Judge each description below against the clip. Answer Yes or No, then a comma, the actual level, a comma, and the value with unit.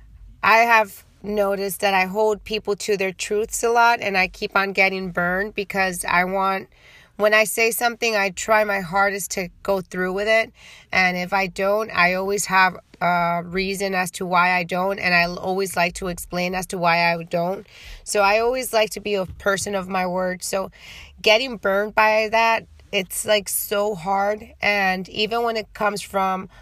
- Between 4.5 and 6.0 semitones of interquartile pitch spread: No, narrow, 2.4 semitones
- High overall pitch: Yes, high, 195 Hz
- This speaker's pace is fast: No, average, 190 wpm